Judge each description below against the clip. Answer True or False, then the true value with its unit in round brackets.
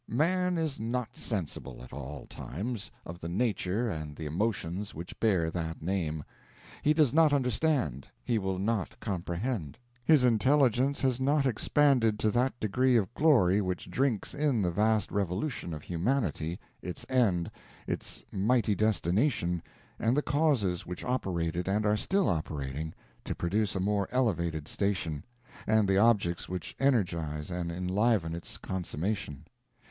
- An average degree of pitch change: False (6.5 semitones)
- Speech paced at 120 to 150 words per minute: True (145 wpm)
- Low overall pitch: True (100 Hz)